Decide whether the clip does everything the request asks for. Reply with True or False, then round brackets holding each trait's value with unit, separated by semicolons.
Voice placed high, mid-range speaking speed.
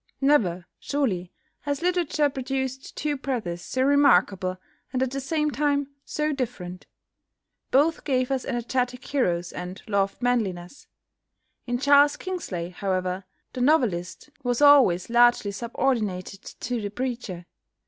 False (245 Hz; 125 wpm)